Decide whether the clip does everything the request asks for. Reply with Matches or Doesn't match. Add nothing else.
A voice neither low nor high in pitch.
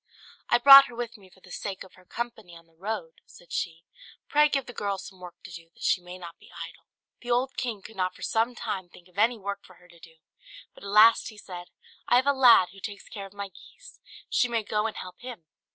Doesn't match